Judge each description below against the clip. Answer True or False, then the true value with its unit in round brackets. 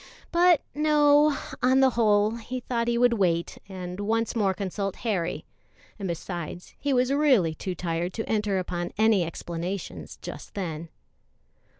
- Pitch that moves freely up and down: True (5.8 semitones)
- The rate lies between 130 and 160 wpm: True (150 wpm)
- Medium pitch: False (205 Hz)